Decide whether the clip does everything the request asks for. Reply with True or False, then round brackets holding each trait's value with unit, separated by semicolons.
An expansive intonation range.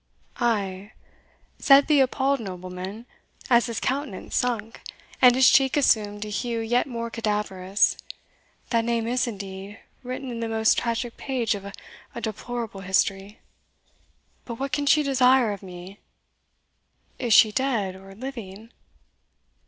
False (4.0 semitones)